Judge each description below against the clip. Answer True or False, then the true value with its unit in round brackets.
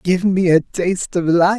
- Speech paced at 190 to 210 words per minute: False (225 wpm)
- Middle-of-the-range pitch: True (180 Hz)